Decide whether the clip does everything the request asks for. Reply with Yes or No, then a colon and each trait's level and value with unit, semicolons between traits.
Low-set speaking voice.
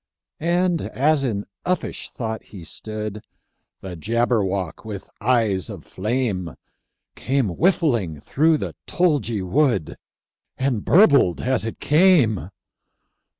Yes: low, 115 Hz